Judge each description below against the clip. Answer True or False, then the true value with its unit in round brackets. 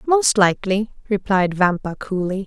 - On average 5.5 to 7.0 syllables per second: False (4.7 syllables/s)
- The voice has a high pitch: True (200 Hz)